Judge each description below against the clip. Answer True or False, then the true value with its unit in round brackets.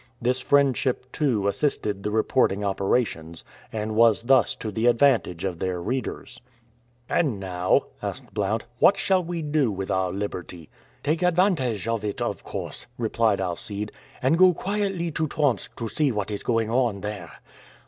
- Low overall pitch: True (115 Hz)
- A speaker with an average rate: True (160 wpm)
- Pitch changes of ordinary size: False (6.2 semitones)